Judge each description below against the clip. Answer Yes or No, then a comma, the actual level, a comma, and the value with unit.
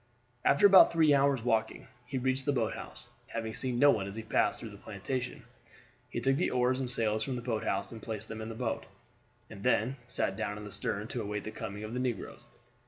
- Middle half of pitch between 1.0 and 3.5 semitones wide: Yes, average, 3.2 semitones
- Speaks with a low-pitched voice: Yes, low, 115 Hz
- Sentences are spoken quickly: Yes, fast, 230 wpm